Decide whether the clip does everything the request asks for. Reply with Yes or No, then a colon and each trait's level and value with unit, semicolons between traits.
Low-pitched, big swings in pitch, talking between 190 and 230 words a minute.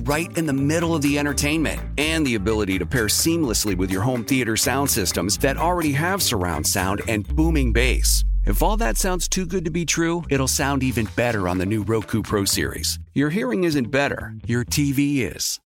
Yes: low, 125 Hz; wide, 6.8 semitones; fast, 205 wpm